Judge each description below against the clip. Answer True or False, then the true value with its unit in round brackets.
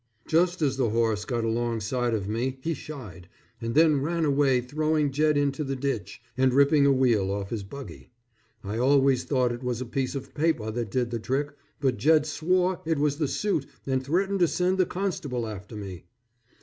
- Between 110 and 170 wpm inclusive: False (200 wpm)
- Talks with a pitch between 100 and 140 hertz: True (135 Hz)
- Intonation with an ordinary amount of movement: True (4.6 semitones)